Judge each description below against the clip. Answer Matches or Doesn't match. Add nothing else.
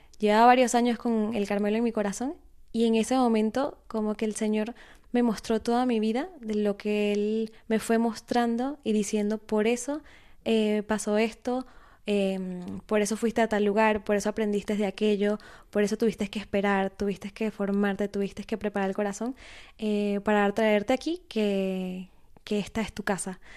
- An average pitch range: Doesn't match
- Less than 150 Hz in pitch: Doesn't match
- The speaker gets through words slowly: Doesn't match